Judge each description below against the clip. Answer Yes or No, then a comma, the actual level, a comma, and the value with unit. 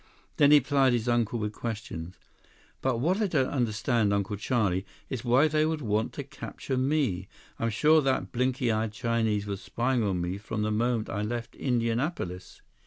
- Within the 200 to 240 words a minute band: No, average, 175 wpm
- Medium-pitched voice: No, low, 115 Hz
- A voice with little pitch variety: No, average, 3.9 semitones